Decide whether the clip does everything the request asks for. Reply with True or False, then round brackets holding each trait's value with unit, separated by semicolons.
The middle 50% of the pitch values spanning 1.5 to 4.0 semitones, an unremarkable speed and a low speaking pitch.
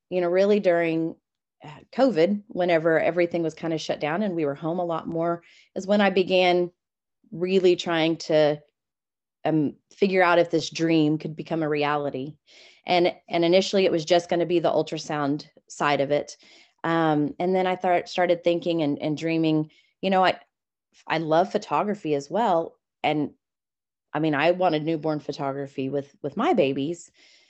False (2.8 semitones; 170 wpm; 165 Hz)